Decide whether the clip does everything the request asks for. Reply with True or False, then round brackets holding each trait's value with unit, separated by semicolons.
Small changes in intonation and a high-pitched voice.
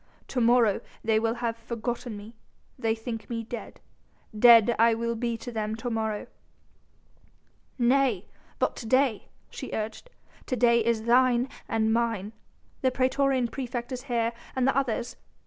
True (1.8 semitones; 235 Hz)